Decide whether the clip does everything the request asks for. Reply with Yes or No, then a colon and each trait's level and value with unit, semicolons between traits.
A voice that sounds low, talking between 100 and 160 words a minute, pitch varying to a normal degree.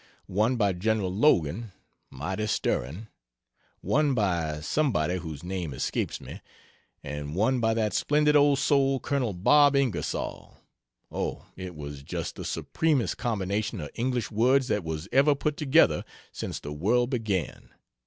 No: low, 110 Hz; average, 140 wpm; wide, 7.3 semitones